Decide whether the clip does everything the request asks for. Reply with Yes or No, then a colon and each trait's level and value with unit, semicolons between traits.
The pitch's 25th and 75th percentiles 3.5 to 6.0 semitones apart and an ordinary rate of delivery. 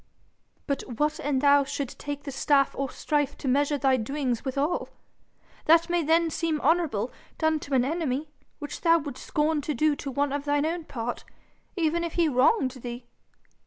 No: average, 2.7 semitones; average, 180 wpm